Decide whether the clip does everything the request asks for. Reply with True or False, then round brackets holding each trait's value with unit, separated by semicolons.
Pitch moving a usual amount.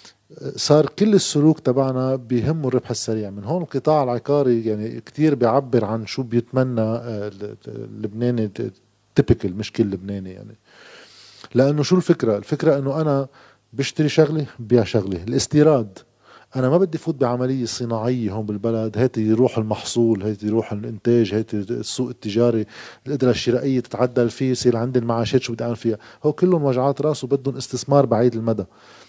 True (3.6 semitones)